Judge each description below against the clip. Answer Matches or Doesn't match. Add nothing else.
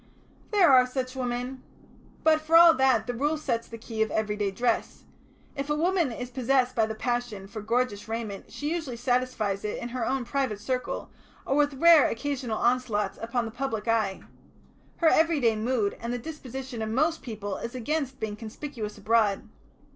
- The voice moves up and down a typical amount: Matches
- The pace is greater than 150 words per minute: Matches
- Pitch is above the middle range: Matches